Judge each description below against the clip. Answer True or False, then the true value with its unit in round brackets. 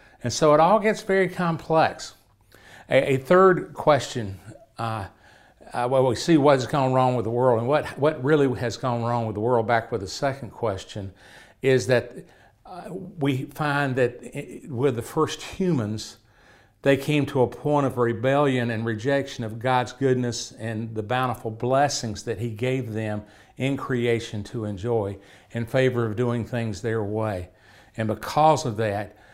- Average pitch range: True (3.9 semitones)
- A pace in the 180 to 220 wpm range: False (170 wpm)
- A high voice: False (125 Hz)